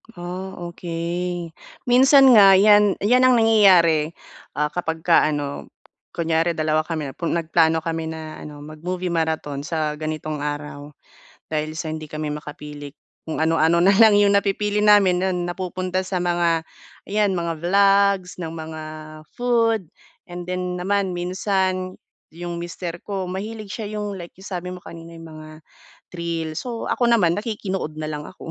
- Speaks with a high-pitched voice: No, medium, 175 Hz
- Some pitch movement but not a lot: Yes, average, 3.6 semitones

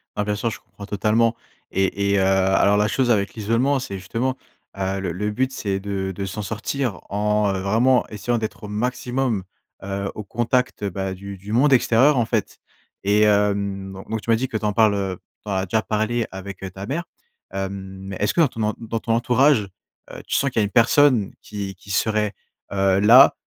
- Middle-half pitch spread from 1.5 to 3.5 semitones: Yes, average, 3.0 semitones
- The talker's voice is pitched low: Yes, low, 105 Hz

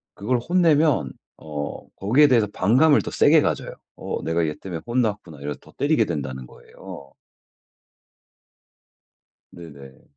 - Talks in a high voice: No, very low, 95 Hz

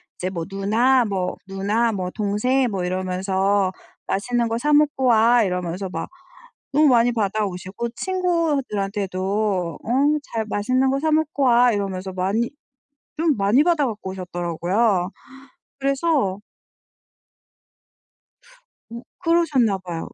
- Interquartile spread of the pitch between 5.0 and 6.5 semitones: Yes, wide, 5.4 semitones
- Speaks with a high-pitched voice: Yes, high, 215 Hz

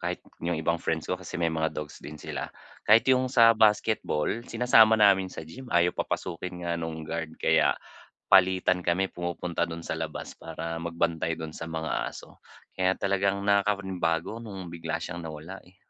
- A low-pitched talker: Yes, very low, 85 Hz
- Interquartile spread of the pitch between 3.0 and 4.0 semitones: Yes, average, 3.3 semitones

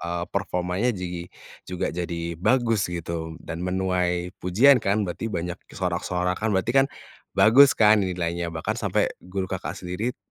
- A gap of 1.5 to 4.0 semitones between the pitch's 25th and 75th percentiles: Yes, narrow, 2.4 semitones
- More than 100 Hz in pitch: No, very low, 90 Hz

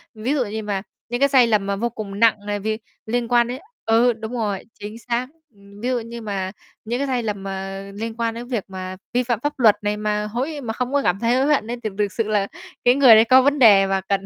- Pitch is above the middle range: Yes, high, 225 Hz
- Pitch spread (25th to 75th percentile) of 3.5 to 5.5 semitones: No, average, 3.1 semitones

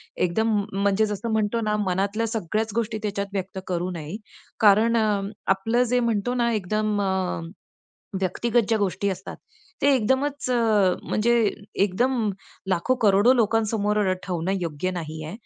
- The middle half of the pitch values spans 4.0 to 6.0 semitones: No, average, 3.2 semitones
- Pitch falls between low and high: No, high, 210 Hz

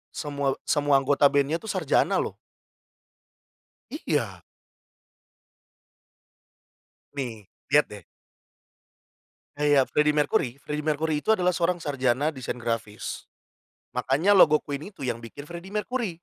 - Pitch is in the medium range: Yes, medium, 145 Hz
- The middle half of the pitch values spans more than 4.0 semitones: No, average, 3.5 semitones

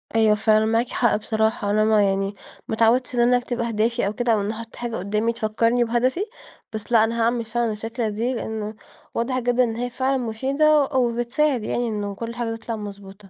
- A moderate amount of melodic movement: No, narrow, 2.1 semitones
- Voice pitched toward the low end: No, high, 230 Hz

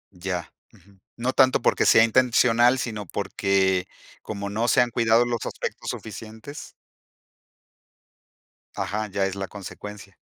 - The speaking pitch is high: No, low, 110 Hz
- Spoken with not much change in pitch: No, average, 3.4 semitones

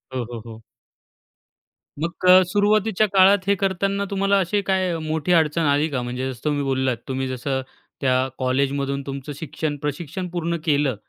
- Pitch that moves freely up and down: Yes, wide, 5.9 semitones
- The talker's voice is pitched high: No, medium, 150 Hz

